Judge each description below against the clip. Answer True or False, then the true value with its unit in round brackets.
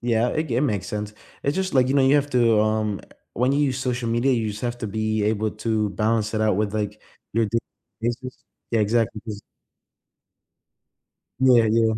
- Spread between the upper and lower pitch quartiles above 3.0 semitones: False (2.6 semitones)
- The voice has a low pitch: True (115 Hz)